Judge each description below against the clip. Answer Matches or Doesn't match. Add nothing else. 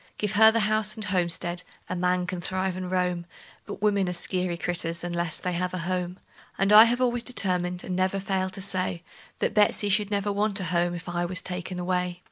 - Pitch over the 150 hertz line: Matches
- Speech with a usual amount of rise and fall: Doesn't match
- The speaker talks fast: Matches